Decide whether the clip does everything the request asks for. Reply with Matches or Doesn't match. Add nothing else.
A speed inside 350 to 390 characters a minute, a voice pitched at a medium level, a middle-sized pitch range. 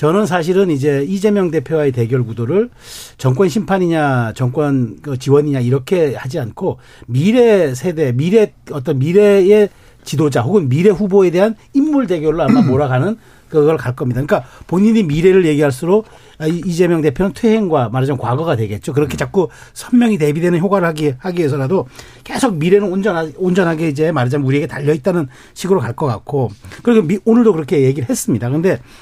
Doesn't match